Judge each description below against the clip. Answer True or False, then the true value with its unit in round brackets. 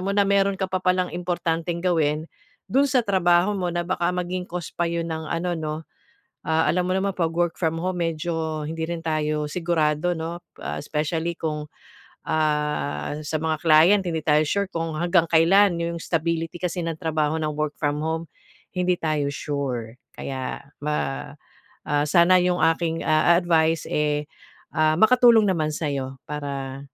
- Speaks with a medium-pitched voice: True (165 Hz)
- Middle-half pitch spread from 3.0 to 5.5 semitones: False (2.6 semitones)